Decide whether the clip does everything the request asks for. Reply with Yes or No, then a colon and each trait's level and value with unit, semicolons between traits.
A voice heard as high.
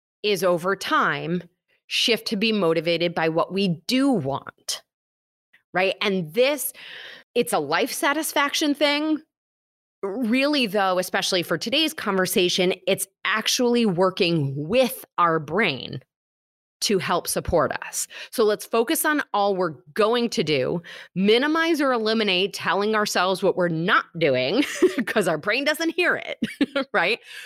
Yes: high, 210 Hz